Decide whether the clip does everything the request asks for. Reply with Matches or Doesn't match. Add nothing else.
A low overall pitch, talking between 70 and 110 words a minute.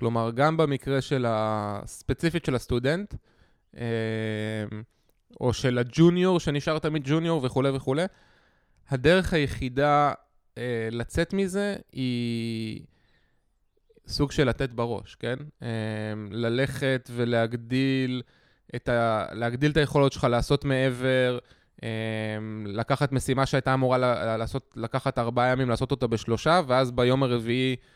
Matches